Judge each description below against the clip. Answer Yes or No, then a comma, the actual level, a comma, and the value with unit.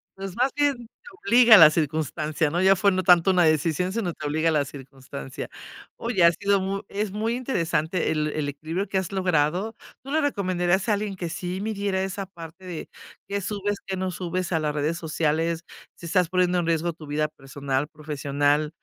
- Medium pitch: Yes, medium, 175 Hz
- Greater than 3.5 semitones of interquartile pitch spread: Yes, average, 4.1 semitones